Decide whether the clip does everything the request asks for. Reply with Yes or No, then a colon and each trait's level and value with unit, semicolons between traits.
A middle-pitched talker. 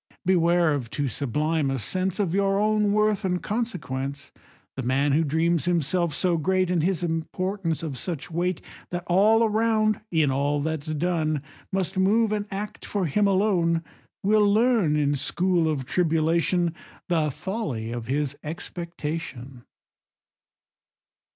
Yes: medium, 170 Hz